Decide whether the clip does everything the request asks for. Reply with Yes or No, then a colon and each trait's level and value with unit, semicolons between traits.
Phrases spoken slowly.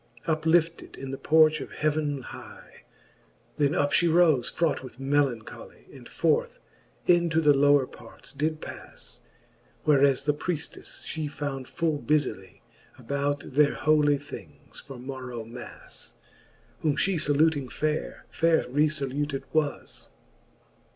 Yes: slow, 125 wpm